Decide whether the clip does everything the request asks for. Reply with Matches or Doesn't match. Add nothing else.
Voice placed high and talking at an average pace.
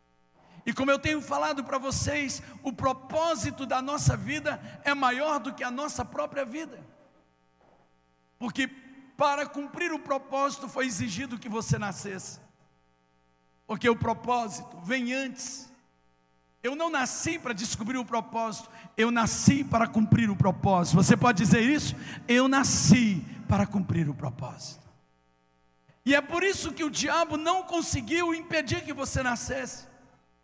Matches